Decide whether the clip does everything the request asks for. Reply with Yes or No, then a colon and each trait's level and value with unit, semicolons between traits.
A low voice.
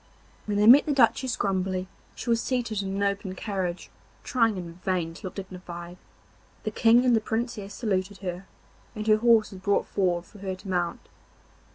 No: high, 195 Hz